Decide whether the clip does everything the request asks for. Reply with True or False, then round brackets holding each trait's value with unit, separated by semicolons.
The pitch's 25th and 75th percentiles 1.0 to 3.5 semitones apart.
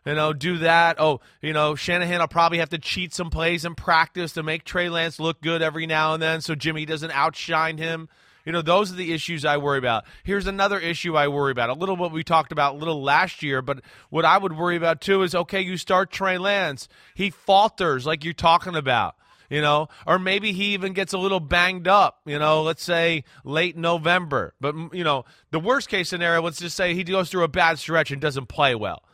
True (2.5 semitones)